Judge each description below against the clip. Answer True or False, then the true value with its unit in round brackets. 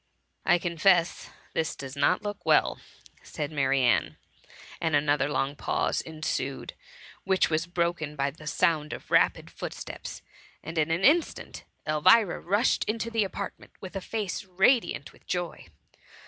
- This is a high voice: False (165 Hz)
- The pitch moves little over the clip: False (4.5 semitones)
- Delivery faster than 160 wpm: False (150 wpm)